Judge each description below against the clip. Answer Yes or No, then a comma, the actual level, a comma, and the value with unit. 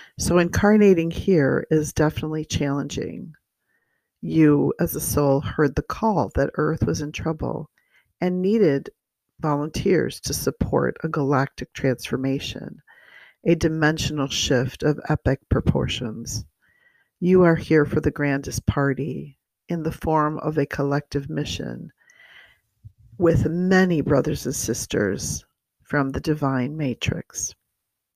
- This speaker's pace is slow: Yes, slow, 115 wpm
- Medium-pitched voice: Yes, medium, 150 Hz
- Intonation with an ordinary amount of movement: Yes, average, 3.1 semitones